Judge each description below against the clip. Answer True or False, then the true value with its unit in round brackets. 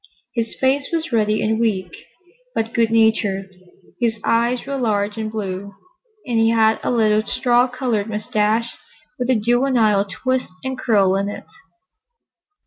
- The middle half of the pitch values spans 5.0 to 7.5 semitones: False (2.6 semitones)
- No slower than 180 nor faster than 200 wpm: False (145 wpm)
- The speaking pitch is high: True (225 Hz)